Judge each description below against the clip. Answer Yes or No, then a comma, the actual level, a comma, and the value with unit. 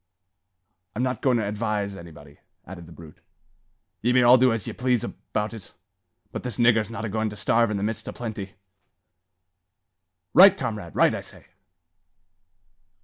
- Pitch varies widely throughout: No, average, 3.4 semitones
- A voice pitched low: Yes, low, 110 Hz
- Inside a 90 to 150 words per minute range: No, average, 165 wpm